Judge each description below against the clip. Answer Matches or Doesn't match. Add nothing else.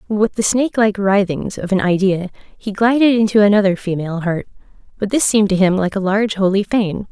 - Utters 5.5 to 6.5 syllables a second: Matches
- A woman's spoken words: Matches